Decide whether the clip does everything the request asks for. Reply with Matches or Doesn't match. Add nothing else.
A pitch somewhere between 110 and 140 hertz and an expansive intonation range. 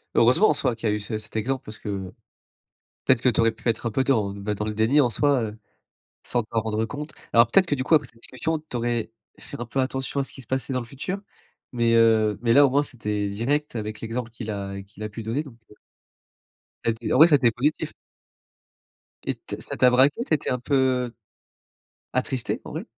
Doesn't match